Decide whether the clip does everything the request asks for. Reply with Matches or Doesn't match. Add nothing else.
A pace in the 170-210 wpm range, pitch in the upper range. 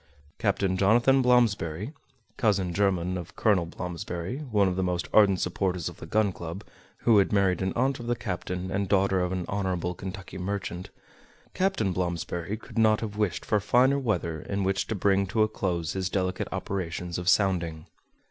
Doesn't match